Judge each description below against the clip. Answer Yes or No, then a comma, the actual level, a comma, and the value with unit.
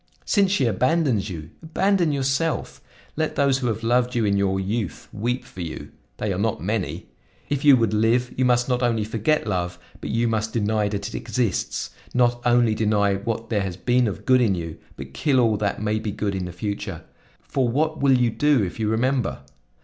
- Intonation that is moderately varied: Yes, average, 4.0 semitones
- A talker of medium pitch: No, low, 115 Hz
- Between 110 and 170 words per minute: No, fast, 205 wpm